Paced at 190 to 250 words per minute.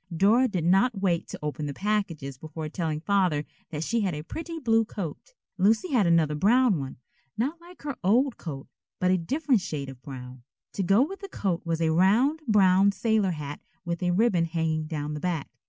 Yes: average, 200 wpm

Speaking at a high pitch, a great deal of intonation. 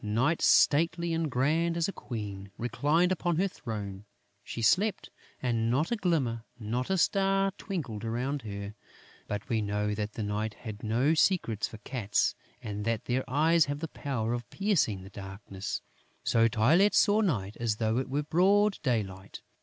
No: low, 125 Hz; wide, 7.5 semitones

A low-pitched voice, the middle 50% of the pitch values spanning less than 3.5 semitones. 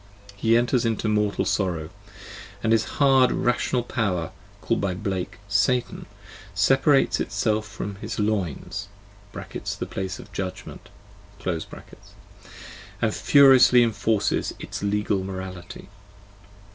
No: low, 105 Hz; average, 4.0 semitones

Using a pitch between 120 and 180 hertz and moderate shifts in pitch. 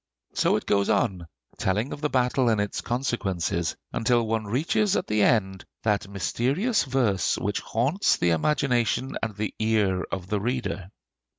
No: low, 110 Hz; average, 4.4 semitones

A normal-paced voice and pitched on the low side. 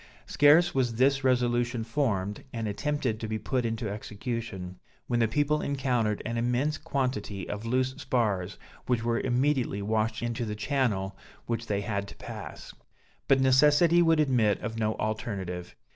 Yes: average, 155 wpm; low, 120 Hz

